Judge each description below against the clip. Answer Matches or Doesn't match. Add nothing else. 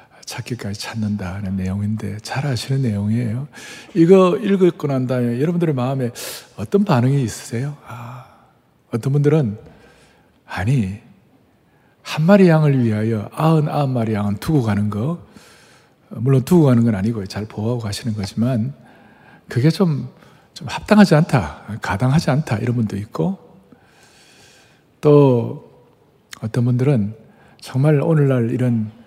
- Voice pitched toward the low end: Matches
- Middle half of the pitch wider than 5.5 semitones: Doesn't match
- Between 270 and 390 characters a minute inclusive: Matches